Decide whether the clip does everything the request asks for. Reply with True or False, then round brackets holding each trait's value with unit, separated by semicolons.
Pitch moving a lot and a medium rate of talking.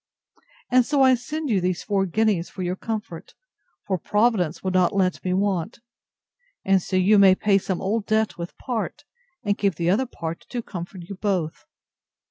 False (3.3 semitones; 180 wpm)